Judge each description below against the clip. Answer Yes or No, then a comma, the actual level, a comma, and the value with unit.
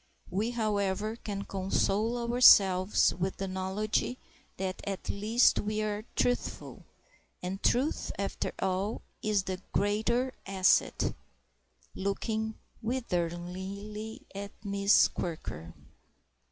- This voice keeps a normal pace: No, slow, 95 wpm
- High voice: Yes, high, 200 Hz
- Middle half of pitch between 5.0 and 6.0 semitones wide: No, narrow, 2.5 semitones